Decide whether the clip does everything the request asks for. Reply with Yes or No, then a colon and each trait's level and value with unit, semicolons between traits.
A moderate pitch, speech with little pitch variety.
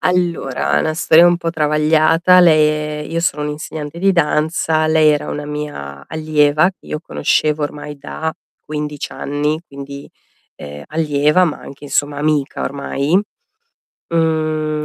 Yes: medium, 150 Hz; narrow, 1.4 semitones